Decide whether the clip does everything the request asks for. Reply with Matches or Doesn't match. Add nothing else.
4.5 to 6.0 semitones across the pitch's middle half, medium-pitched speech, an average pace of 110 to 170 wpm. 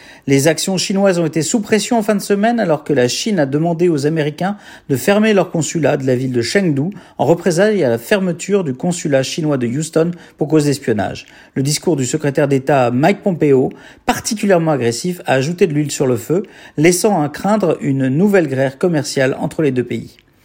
Doesn't match